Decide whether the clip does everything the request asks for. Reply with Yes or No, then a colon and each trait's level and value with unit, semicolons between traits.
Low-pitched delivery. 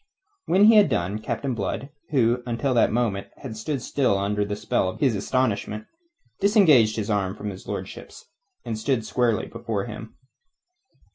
Yes: low, 115 Hz